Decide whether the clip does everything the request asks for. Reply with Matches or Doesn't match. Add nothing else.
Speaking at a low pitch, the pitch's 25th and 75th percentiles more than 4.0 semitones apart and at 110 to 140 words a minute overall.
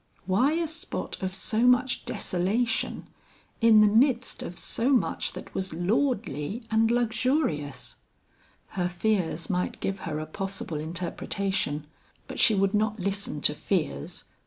Doesn't match